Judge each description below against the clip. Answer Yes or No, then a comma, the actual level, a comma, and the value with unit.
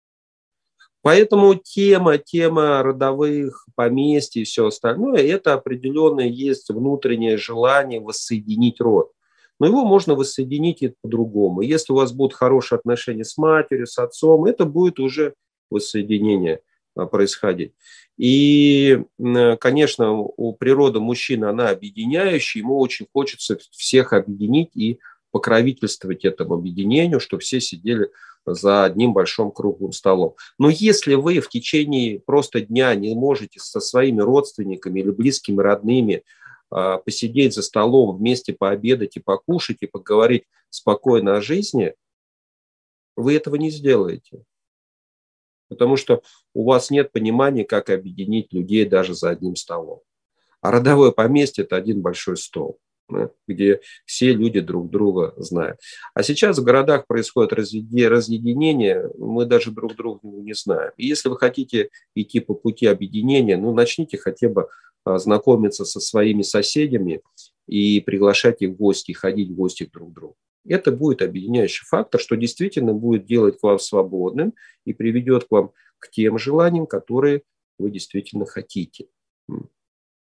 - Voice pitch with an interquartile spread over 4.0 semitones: Yes, wide, 5.5 semitones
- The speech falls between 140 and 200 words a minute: No, average, 130 wpm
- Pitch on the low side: Yes, low, 125 Hz